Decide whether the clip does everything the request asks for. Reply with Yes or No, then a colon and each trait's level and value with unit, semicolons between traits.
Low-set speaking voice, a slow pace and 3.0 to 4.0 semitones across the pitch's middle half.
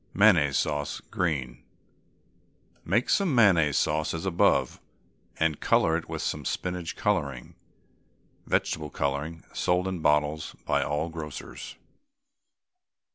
Yes: very low, 80 Hz; slow, 110 wpm; average, 3.6 semitones